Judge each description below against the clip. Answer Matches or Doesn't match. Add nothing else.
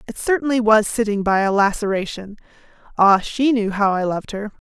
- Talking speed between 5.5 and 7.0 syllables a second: Matches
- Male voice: Doesn't match